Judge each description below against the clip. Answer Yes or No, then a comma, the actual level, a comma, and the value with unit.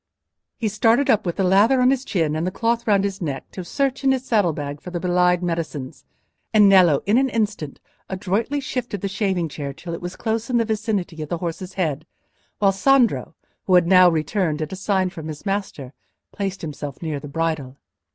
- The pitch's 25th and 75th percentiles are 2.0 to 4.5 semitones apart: No, average, 4.9 semitones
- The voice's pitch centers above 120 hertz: Yes, medium, 185 Hz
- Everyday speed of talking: No, fast, 210 wpm